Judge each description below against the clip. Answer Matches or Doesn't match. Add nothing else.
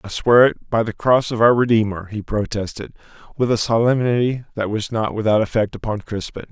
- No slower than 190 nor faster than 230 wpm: Matches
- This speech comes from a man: Matches